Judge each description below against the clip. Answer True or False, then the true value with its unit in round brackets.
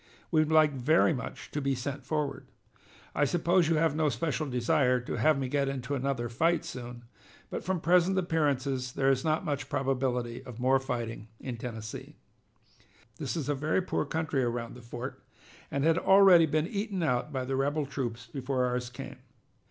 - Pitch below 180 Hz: True (135 Hz)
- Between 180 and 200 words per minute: True (185 wpm)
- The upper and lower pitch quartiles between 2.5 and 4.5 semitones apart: True (3.9 semitones)